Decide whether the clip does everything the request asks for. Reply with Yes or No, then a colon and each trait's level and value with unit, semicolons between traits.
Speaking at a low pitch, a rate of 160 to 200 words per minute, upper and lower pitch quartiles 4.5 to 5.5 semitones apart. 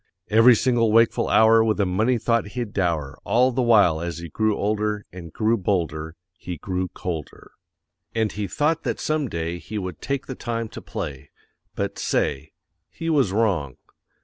Yes: low, 105 Hz; average, 175 wpm; average, 5.0 semitones